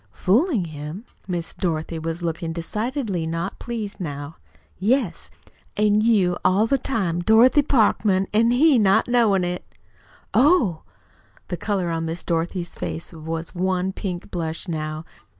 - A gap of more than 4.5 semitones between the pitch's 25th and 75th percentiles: Yes, average, 5.0 semitones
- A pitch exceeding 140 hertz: Yes, medium, 185 Hz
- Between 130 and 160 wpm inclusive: Yes, slow, 135 wpm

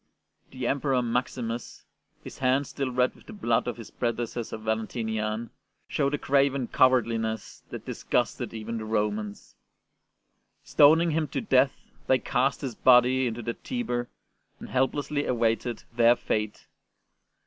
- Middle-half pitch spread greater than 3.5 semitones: No, average, 2.9 semitones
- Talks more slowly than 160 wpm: Yes, average, 145 wpm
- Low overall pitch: Yes, low, 120 Hz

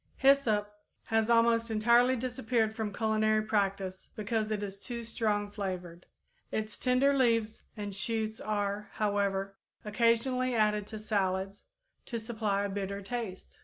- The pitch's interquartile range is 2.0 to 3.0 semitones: Yes, narrow, 2.4 semitones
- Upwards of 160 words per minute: No, slow, 135 wpm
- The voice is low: No, high, 215 Hz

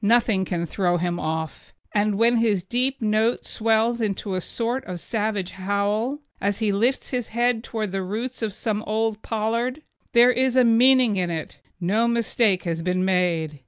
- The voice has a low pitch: No, high, 215 Hz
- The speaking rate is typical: Yes, average, 180 wpm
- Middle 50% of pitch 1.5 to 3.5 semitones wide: No, average, 4.0 semitones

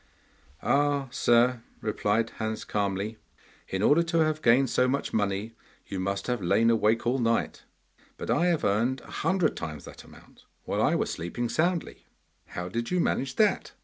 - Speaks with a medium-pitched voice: No, low, 115 Hz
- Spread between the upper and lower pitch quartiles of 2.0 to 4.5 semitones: No, average, 5.2 semitones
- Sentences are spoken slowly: No, average, 170 wpm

